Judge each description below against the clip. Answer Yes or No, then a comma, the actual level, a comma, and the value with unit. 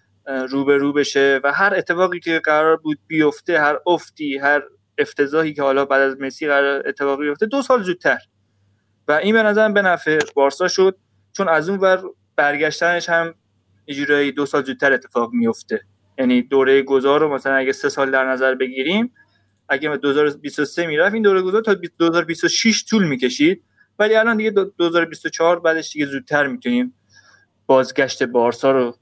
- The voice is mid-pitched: Yes, medium, 145 Hz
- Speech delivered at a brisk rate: Yes, fast, 165 wpm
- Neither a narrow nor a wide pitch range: Yes, average, 4.2 semitones